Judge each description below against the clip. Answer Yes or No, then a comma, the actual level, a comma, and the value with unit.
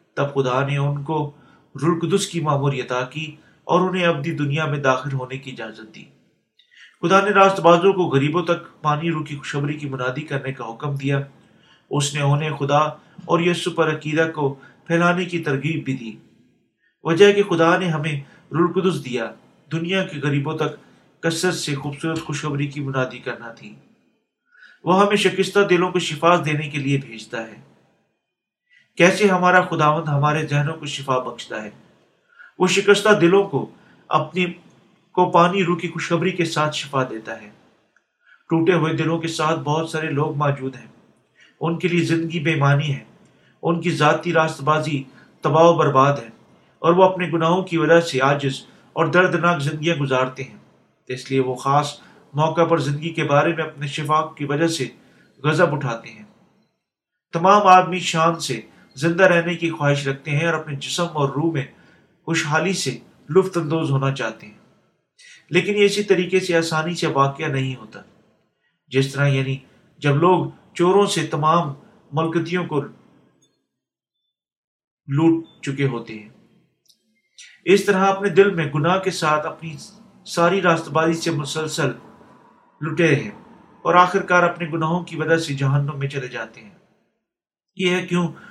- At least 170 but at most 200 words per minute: No, average, 160 wpm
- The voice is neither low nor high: Yes, medium, 160 Hz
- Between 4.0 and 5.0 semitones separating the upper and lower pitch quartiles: No, average, 3.5 semitones